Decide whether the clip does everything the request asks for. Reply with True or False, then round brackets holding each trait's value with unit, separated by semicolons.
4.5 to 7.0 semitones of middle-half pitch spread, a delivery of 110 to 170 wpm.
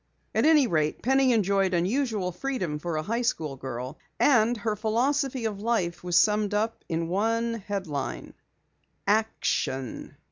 True (5.3 semitones; 140 wpm)